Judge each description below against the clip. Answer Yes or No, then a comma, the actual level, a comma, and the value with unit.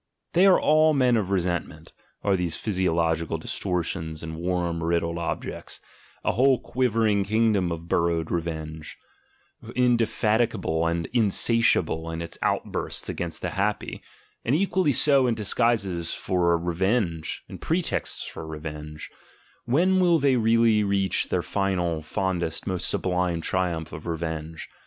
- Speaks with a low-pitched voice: Yes, very low, 90 Hz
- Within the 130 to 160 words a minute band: Yes, average, 140 wpm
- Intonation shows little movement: No, wide, 5.6 semitones